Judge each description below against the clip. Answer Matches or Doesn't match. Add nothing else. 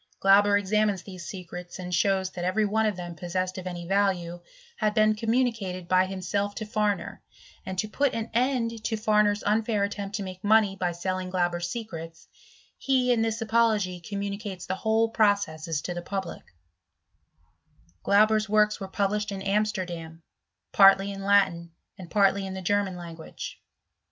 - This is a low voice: Doesn't match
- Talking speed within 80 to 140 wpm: Doesn't match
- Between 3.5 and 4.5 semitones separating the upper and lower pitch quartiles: Doesn't match